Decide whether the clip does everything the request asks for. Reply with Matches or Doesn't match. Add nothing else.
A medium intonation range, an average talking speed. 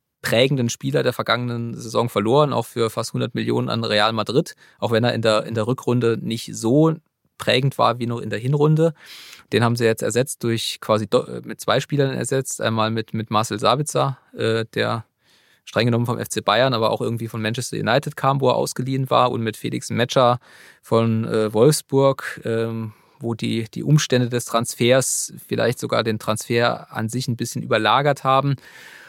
Matches